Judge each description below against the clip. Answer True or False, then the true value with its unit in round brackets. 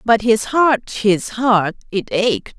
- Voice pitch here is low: False (220 Hz)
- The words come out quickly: False (165 wpm)